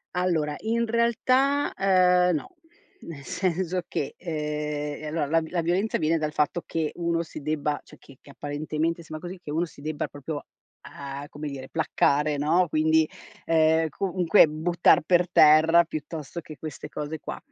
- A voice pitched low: No, medium, 160 Hz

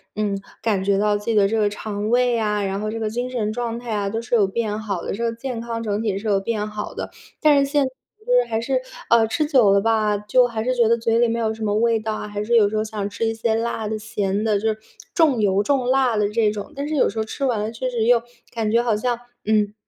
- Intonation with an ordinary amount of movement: No, narrow, 2.1 semitones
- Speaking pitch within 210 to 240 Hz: Yes, high, 220 Hz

